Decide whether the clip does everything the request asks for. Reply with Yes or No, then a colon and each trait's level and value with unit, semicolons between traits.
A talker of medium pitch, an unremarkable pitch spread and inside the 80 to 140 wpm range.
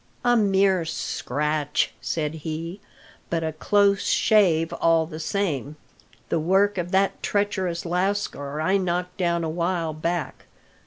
Yes: medium, 170 Hz; average, 3.4 semitones; slow, 135 wpm